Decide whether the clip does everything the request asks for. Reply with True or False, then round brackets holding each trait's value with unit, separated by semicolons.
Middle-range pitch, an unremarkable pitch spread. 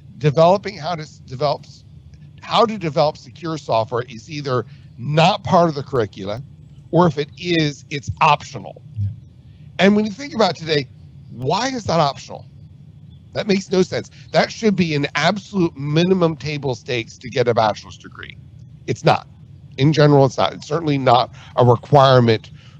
True (145 Hz; 4.2 semitones)